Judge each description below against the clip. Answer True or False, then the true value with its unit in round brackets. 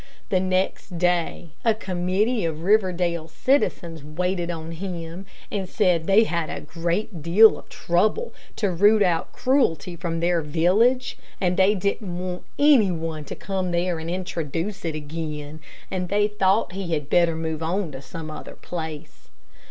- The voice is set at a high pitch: False (175 Hz)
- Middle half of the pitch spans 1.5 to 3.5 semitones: True (3.1 semitones)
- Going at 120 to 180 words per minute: True (160 wpm)